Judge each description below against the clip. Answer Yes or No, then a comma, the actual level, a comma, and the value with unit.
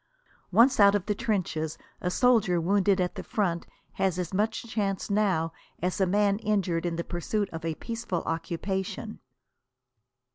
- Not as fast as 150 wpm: No, average, 155 wpm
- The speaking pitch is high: Yes, high, 195 Hz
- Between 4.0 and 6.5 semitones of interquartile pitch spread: No, average, 3.3 semitones